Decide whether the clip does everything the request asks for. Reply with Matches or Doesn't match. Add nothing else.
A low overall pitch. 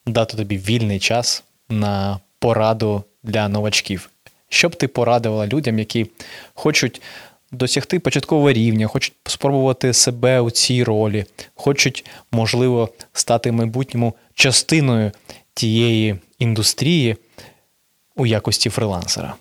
Matches